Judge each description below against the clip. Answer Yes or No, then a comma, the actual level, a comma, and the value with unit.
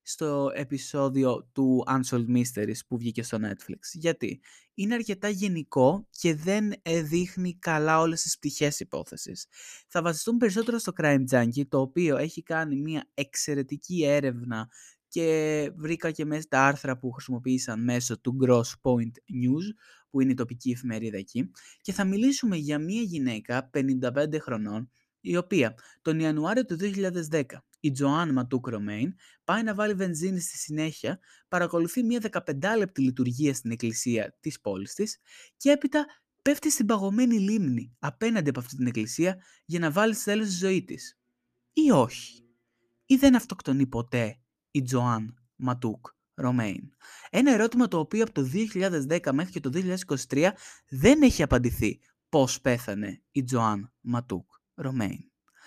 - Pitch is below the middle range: No, medium, 145 Hz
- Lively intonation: Yes, wide, 6.8 semitones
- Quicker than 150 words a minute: No, average, 145 wpm